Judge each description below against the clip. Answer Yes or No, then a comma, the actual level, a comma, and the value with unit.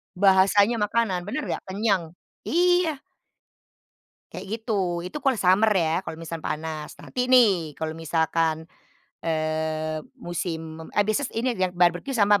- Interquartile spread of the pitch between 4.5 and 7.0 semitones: Yes, average, 5.2 semitones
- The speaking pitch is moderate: Yes, medium, 180 Hz